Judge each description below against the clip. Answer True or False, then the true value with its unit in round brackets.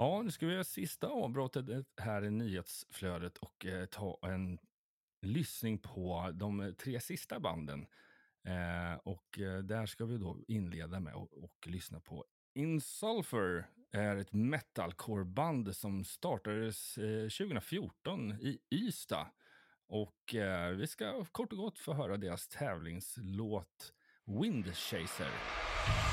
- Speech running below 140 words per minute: True (125 wpm)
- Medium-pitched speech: False (105 Hz)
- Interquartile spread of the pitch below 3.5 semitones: False (4.2 semitones)